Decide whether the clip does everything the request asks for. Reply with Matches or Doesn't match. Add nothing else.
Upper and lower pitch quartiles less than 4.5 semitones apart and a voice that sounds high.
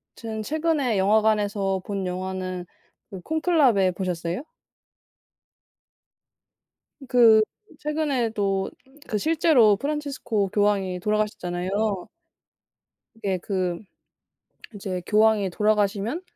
Matches